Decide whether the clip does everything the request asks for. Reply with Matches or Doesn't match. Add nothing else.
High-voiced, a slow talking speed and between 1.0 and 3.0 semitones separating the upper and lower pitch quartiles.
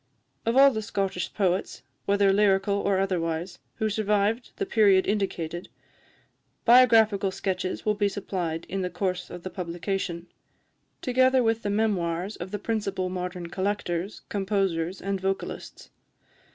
Matches